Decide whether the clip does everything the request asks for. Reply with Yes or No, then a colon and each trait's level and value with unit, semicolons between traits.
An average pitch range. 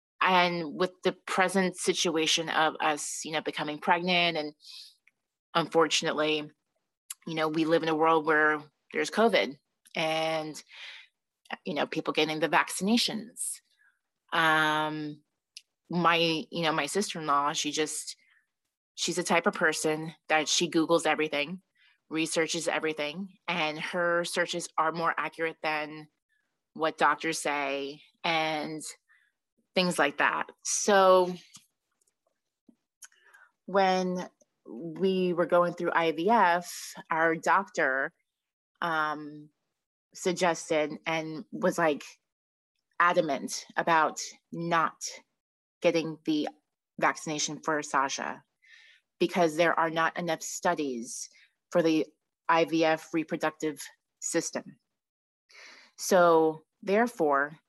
No: narrow, 2.2 semitones